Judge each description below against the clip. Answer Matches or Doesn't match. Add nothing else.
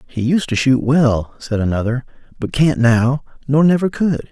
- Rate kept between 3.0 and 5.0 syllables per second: Matches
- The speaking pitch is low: Matches